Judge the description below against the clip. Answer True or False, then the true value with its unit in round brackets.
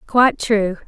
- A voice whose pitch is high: True (220 Hz)